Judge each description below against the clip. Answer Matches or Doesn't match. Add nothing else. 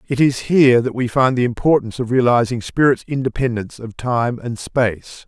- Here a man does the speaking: Matches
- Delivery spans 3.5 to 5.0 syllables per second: Doesn't match